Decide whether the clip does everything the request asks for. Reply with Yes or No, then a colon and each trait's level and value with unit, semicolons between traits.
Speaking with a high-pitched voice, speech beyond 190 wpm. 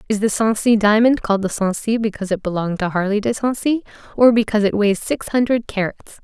Yes: high, 215 Hz; average, 200 wpm